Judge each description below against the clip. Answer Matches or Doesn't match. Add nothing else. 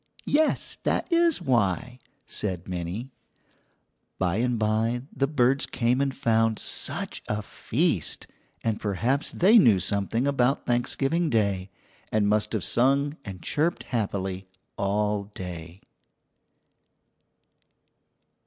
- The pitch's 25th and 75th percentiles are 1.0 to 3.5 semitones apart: Doesn't match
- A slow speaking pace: Matches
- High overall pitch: Doesn't match